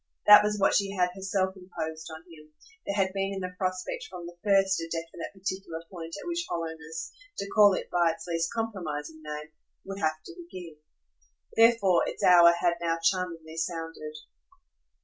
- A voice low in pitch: No, medium, 175 Hz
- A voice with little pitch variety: No, average, 3.0 semitones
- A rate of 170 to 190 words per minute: Yes, average, 175 wpm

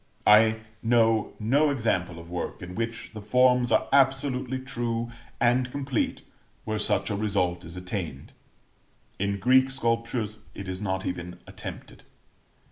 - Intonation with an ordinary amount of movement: Yes, average, 4.8 semitones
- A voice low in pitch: Yes, low, 110 Hz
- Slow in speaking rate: Yes, slow, 130 wpm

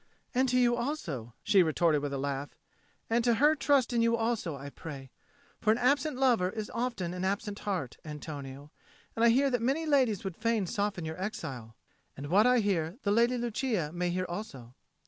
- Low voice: No, high, 205 Hz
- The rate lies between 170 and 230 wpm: Yes, average, 195 wpm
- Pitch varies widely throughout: Yes, wide, 7.2 semitones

